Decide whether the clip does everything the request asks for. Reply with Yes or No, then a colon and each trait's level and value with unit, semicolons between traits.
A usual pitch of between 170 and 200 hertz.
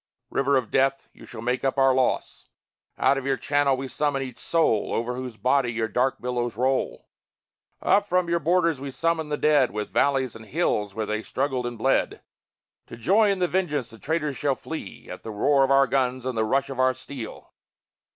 No: low, 135 Hz